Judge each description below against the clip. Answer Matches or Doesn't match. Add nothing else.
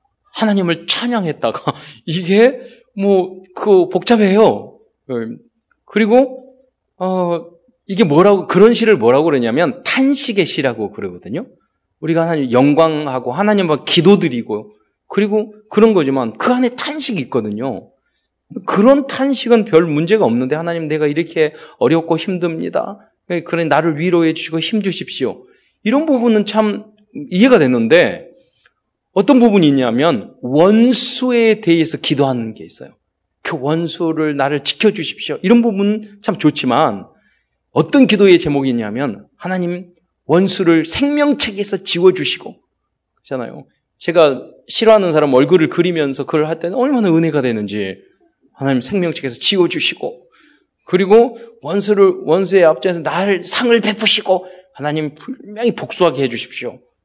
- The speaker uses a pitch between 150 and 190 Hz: Matches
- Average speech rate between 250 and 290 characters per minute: Doesn't match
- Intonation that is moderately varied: Doesn't match